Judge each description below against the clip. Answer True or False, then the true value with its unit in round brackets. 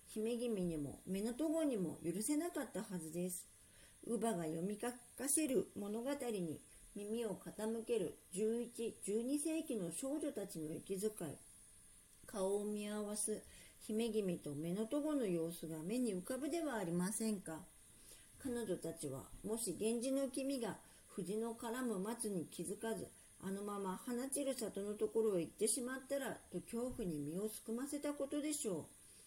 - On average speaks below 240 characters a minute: False (285 characters per minute)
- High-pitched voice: True (215 Hz)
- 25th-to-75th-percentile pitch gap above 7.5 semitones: False (5.5 semitones)